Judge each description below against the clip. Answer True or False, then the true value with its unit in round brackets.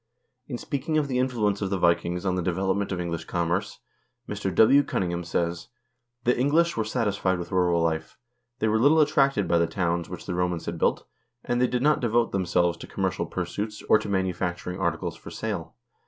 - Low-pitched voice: True (95 Hz)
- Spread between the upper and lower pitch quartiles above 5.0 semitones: True (5.6 semitones)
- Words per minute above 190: True (200 wpm)